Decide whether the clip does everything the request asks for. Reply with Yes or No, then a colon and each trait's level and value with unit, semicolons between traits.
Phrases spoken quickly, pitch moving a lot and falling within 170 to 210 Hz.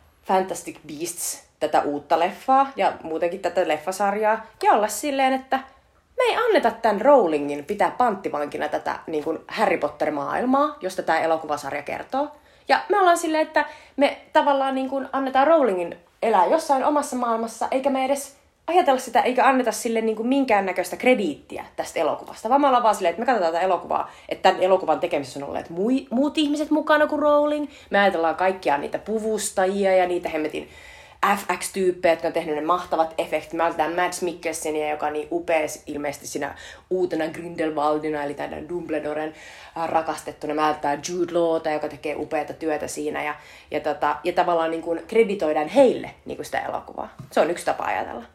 Yes: fast, 170 wpm; wide, 8.9 semitones; medium, 185 Hz